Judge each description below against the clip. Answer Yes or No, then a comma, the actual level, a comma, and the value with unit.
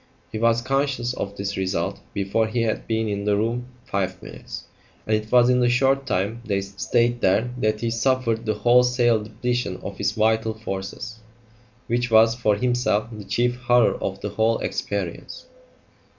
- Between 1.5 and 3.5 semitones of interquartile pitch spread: Yes, average, 2.9 semitones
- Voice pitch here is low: Yes, low, 115 Hz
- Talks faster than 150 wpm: Yes, average, 170 wpm